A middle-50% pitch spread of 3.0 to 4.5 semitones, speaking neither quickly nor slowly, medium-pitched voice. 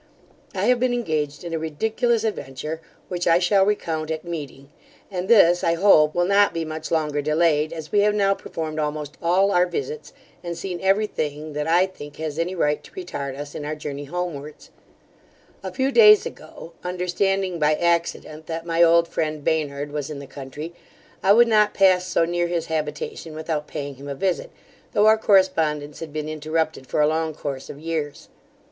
Yes: average, 3.7 semitones; average, 190 wpm; medium, 165 Hz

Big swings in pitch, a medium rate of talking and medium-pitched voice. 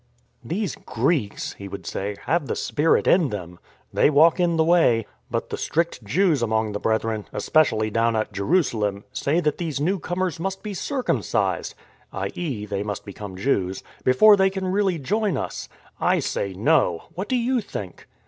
Yes: wide, 9.0 semitones; average, 185 wpm; medium, 145 Hz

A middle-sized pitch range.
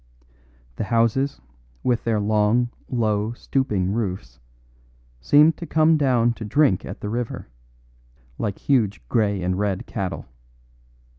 Yes: average, 3.6 semitones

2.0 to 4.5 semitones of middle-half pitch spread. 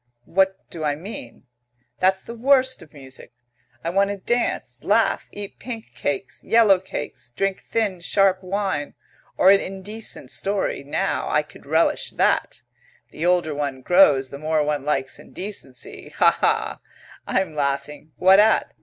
No: average, 5.2 semitones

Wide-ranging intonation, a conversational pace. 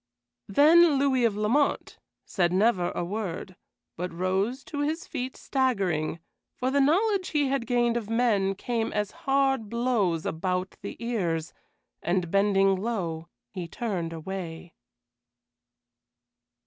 No: wide, 6.1 semitones; slow, 125 wpm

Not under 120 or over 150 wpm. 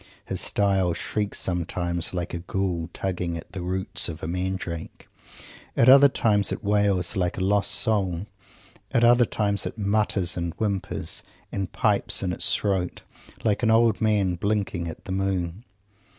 No: average, 160 wpm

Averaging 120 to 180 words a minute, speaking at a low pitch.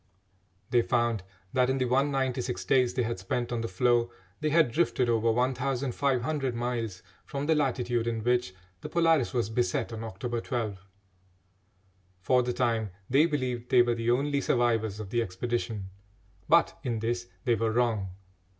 Yes: average, 160 wpm; low, 120 Hz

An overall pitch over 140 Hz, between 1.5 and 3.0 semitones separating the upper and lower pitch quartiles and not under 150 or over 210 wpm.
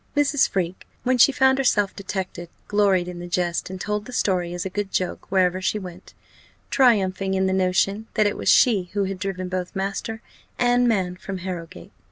Yes: high, 190 Hz; narrow, 2.4 semitones; average, 195 wpm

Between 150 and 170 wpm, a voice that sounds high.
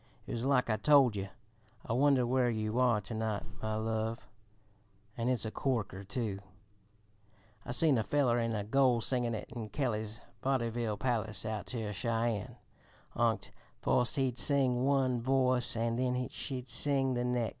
No: average, 165 wpm; low, 120 Hz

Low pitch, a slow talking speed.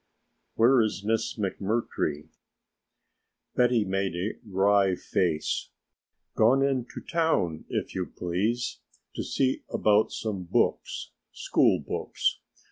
Yes: low, 105 Hz; slow, 105 wpm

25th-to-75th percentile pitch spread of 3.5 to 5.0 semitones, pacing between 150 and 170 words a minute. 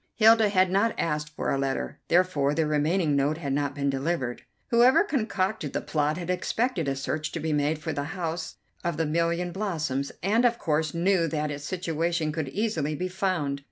No: average, 4.0 semitones; average, 190 wpm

